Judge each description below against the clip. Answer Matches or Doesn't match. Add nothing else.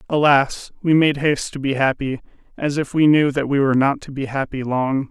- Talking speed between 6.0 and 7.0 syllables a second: Doesn't match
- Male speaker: Matches